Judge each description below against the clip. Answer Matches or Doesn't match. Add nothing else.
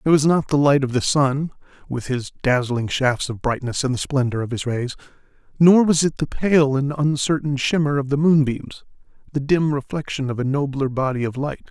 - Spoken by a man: Matches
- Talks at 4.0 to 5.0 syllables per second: Doesn't match